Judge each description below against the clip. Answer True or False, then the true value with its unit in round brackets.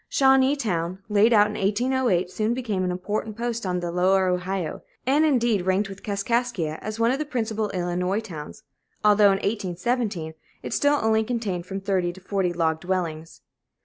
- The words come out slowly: False (170 wpm)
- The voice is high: True (200 Hz)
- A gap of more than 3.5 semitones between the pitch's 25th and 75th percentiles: True (4.2 semitones)